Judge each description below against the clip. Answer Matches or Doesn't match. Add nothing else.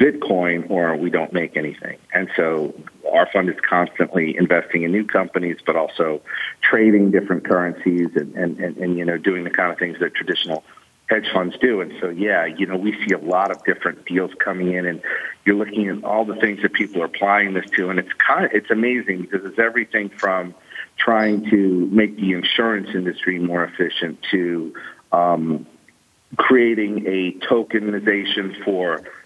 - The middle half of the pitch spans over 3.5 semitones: Doesn't match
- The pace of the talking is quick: Doesn't match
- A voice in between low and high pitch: Doesn't match